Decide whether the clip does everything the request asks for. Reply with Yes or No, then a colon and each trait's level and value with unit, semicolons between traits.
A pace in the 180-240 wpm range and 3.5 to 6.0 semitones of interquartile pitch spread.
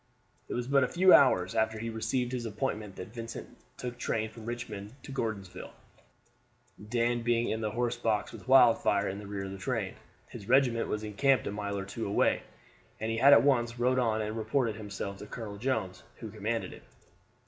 No: average, 195 wpm; average, 2.8 semitones